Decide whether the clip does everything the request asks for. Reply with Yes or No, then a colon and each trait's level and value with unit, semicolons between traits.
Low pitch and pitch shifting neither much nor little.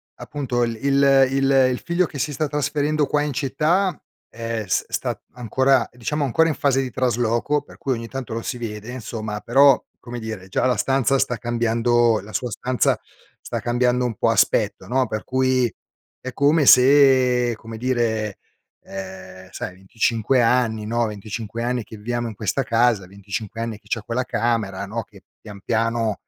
Yes: low, 120 Hz; average, 3.1 semitones